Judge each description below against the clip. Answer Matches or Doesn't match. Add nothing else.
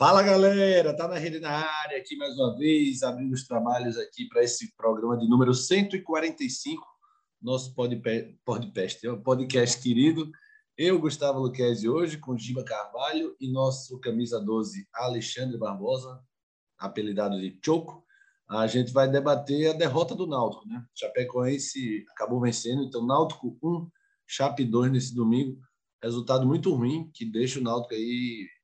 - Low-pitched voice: Matches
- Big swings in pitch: Matches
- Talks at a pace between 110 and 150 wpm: Matches